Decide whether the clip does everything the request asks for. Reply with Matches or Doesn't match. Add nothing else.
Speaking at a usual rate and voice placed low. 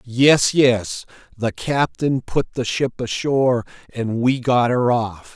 Matches